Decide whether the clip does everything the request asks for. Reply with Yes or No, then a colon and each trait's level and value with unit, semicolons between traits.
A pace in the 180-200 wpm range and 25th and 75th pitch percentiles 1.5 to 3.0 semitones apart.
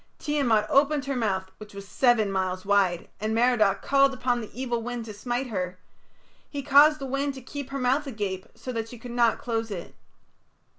No: average, 195 wpm; average, 4.6 semitones